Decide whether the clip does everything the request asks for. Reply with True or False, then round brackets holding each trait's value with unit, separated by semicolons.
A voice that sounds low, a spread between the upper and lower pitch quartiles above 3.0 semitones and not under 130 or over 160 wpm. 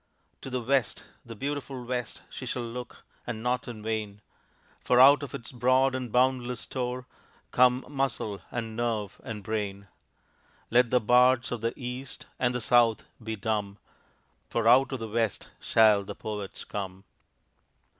False (120 Hz; 2.6 semitones; 155 wpm)